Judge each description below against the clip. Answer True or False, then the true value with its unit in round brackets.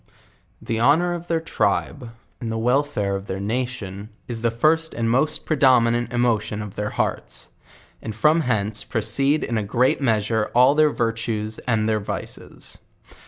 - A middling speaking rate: True (160 wpm)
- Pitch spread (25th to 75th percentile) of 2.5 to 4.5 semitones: True (4.0 semitones)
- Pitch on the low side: True (115 Hz)